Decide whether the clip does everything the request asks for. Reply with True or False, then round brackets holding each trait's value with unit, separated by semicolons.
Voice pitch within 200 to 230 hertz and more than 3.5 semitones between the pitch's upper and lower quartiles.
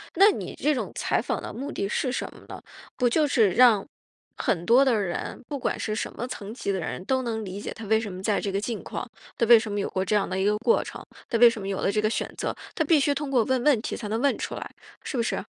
True (225 Hz; 4.4 semitones)